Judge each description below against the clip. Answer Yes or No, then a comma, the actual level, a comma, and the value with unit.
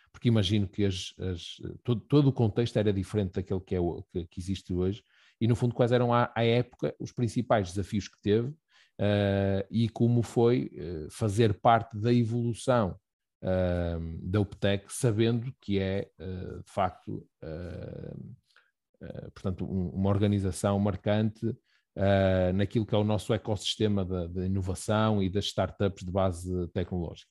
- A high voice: No, low, 100 Hz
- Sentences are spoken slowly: No, average, 160 wpm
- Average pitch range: Yes, average, 3.6 semitones